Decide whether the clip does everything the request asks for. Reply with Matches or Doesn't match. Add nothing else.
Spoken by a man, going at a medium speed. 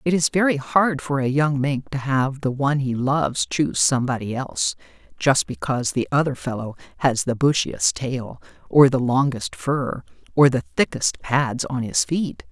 Doesn't match